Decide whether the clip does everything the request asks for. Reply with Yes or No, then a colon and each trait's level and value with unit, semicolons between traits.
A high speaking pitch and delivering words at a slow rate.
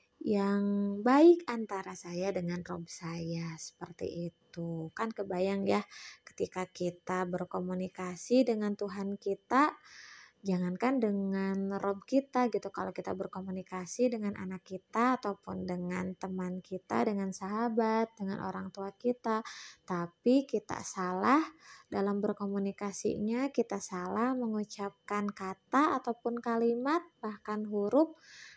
No: high, 200 Hz; average, 110 wpm